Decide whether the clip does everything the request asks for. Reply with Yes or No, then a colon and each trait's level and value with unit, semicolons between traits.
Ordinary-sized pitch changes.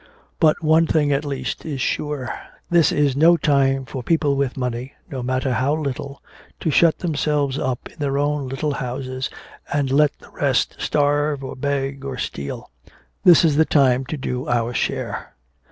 No: narrow, 2.3 semitones